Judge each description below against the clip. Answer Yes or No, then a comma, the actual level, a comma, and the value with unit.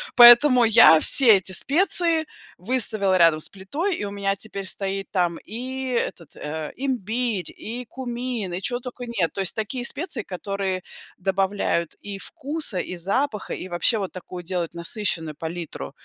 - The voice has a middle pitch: No, high, 200 Hz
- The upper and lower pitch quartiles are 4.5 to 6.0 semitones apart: Yes, average, 5.2 semitones